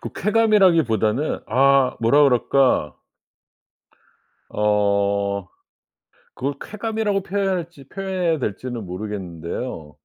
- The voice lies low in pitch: Yes, low, 130 Hz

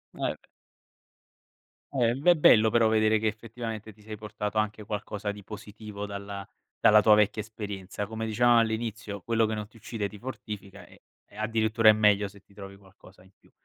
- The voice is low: Yes, low, 105 Hz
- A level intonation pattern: Yes, narrow, 1.5 semitones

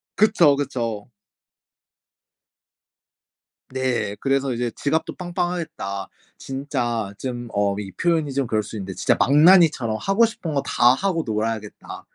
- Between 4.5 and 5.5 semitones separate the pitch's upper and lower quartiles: No, wide, 6.5 semitones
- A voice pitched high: No, low, 130 Hz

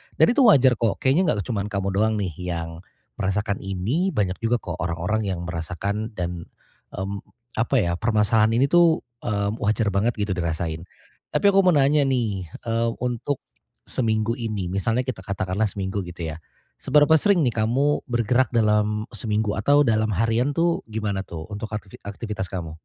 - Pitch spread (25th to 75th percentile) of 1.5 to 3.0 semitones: No, average, 4.0 semitones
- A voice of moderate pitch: No, low, 105 Hz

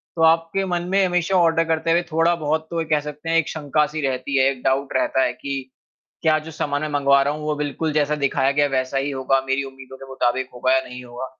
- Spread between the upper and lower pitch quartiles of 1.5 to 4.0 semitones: Yes, average, 3.3 semitones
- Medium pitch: Yes, medium, 145 Hz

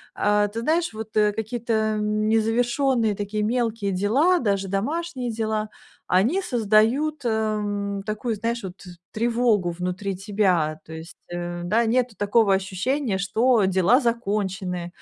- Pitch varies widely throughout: No, average, 3.2 semitones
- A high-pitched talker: Yes, high, 215 Hz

